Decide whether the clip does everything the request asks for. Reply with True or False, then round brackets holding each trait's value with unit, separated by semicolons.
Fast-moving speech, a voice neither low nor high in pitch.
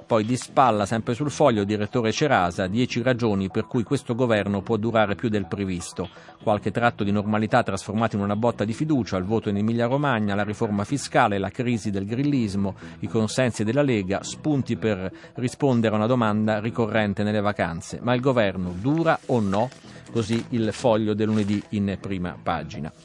False (175 wpm; 110 Hz)